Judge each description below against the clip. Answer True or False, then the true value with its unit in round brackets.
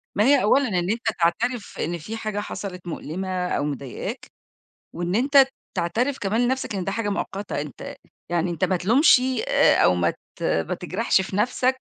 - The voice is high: True (200 Hz)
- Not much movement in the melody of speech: False (5.6 semitones)